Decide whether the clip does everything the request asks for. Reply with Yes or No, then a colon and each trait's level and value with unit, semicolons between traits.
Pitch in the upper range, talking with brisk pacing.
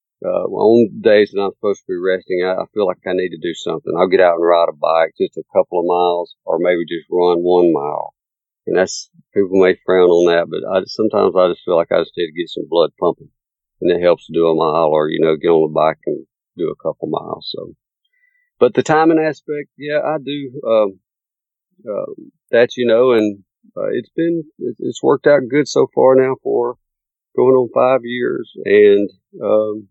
No: low, 120 Hz; fast, 220 wpm